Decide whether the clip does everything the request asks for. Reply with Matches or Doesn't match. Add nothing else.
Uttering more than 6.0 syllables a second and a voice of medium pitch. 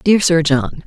Doesn't match